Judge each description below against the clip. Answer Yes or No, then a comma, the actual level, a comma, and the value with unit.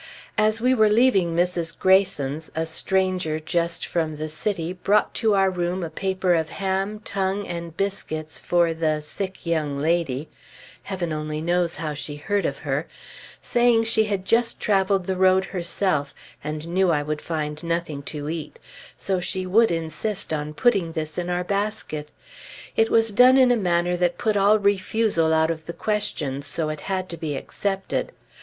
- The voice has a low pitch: No, medium, 175 Hz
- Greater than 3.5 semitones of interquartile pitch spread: Yes, average, 3.9 semitones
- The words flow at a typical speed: Yes, average, 175 wpm